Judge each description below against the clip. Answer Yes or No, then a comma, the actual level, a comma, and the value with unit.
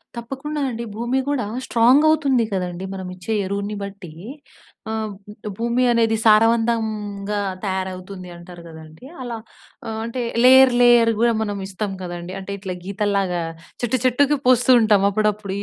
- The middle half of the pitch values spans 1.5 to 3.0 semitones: No, average, 3.7 semitones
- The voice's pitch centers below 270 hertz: Yes, high, 215 Hz